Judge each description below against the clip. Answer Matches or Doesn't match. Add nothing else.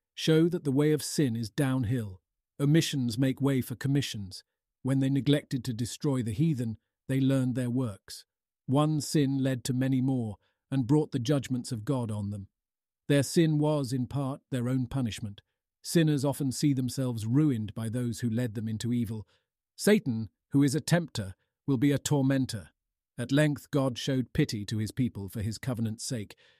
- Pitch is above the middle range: Doesn't match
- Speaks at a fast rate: Doesn't match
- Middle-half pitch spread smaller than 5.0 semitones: Matches